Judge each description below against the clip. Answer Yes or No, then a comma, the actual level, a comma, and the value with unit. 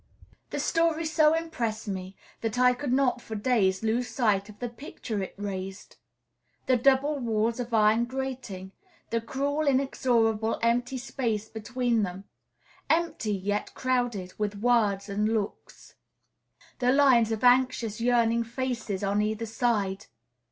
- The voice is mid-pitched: No, high, 230 Hz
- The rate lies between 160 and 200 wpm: No, slow, 135 wpm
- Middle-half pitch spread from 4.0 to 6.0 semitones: No, average, 3.4 semitones